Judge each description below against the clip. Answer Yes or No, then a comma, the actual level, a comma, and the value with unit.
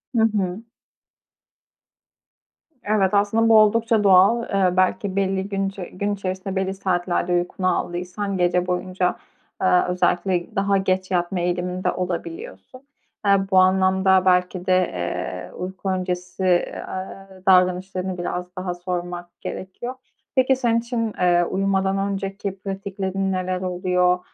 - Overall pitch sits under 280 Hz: Yes, medium, 185 Hz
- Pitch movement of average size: No, narrow, 1.5 semitones